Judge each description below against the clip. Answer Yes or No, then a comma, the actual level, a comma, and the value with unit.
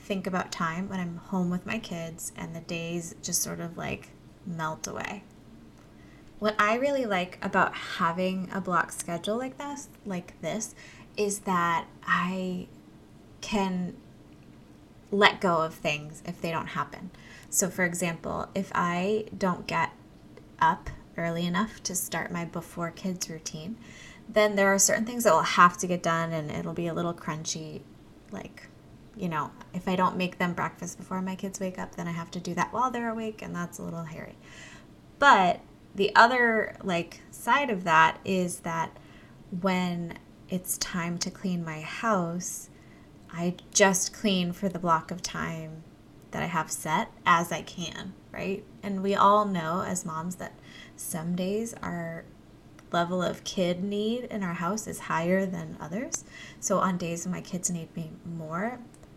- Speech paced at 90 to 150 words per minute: No, average, 170 wpm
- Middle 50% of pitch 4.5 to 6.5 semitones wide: No, average, 2.8 semitones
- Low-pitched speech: No, medium, 180 Hz